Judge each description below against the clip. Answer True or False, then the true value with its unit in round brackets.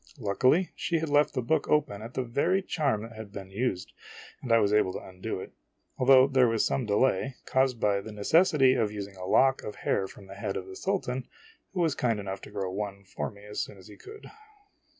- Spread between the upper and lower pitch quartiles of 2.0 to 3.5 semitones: False (5.0 semitones)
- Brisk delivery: True (230 wpm)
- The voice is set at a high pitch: False (115 Hz)